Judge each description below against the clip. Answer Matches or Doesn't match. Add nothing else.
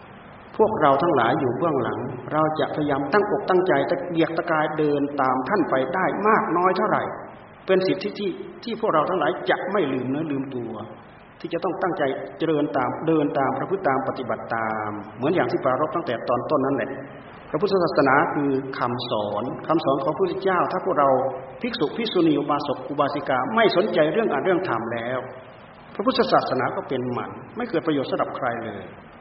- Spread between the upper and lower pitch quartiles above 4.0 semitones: Matches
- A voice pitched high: Doesn't match